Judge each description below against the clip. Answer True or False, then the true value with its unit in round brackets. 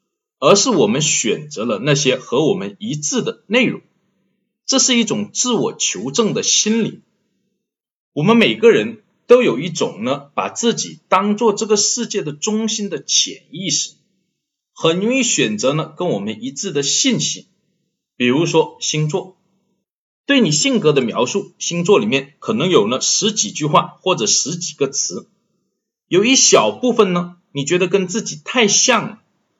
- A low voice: False (205 Hz)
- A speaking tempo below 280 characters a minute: True (230 characters per minute)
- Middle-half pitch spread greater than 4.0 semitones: True (4.5 semitones)